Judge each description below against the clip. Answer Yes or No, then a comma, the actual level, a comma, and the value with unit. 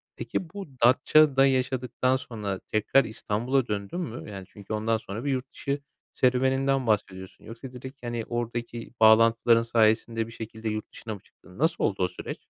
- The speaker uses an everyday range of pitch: Yes, average, 3.3 semitones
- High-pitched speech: No, low, 115 Hz